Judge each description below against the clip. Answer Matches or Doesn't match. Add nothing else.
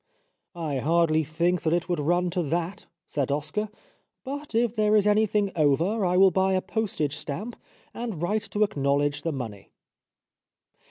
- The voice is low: Doesn't match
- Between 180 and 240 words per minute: Doesn't match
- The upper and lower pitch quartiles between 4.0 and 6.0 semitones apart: Matches